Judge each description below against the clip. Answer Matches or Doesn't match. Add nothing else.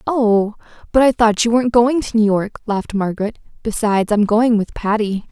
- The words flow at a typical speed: Matches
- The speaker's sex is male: Doesn't match